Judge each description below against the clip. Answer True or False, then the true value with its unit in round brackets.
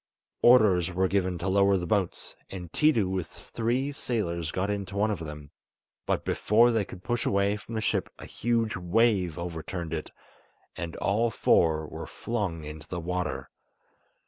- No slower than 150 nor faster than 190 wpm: True (165 wpm)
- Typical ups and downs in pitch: True (4.2 semitones)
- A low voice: True (95 Hz)